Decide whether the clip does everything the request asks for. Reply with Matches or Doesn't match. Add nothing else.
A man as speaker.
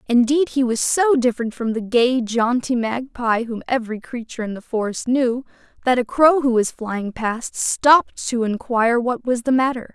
Doesn't match